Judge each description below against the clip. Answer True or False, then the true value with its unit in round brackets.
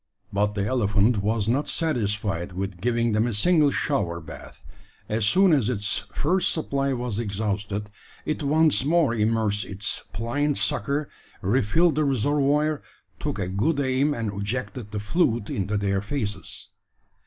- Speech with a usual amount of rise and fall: False (5.7 semitones)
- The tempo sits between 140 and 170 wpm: True (150 wpm)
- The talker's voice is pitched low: True (115 Hz)